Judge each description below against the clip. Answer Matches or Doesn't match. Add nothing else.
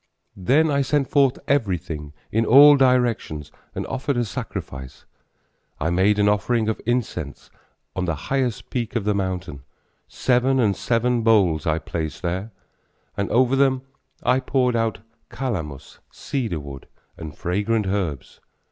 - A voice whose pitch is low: Matches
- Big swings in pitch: Matches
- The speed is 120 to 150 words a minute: Matches